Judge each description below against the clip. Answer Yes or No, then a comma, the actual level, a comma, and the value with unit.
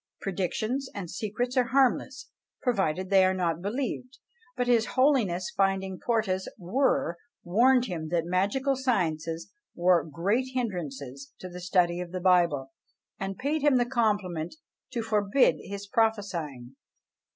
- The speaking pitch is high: Yes, high, 195 Hz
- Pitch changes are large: Yes, wide, 5.8 semitones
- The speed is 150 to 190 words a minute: No, slow, 135 wpm